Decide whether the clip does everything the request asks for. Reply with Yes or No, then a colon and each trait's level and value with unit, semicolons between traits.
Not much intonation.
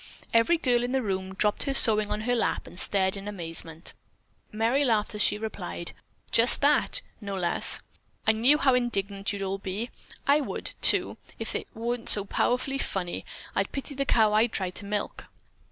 No: average, 3.9 semitones